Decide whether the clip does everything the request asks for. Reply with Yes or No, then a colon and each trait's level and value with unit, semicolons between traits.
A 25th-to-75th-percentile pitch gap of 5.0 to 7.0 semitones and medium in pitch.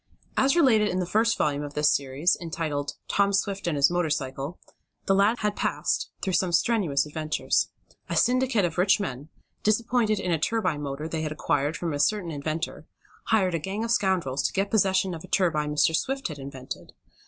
Yes: wide, 5.6 semitones; medium, 175 Hz